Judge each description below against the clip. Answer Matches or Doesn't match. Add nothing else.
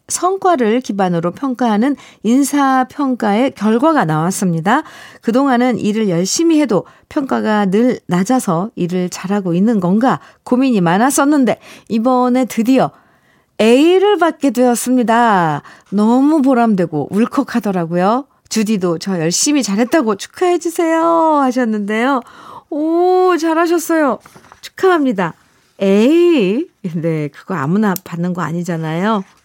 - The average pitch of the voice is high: Matches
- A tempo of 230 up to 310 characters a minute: Matches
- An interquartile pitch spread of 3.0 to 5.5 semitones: Doesn't match